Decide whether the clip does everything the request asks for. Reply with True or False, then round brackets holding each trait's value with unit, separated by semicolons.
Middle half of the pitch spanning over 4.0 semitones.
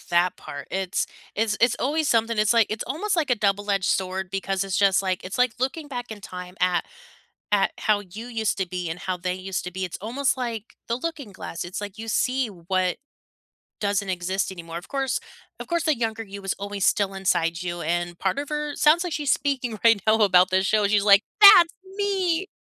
True (5.0 semitones)